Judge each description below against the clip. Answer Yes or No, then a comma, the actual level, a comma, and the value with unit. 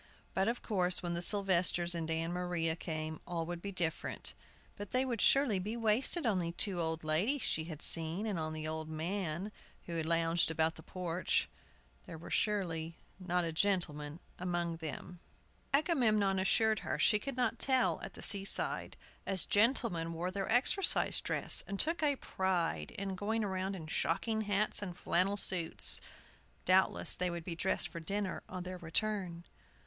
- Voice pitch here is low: No, medium, 180 Hz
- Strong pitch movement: No, average, 3.7 semitones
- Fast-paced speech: No, average, 175 wpm